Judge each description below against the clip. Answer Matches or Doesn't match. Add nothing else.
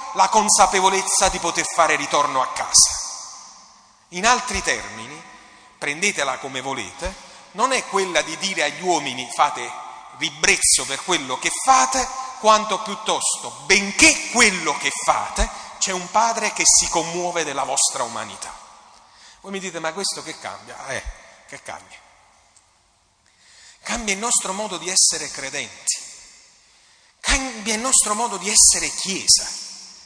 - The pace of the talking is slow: Doesn't match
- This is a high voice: Matches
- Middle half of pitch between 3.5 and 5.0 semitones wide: Matches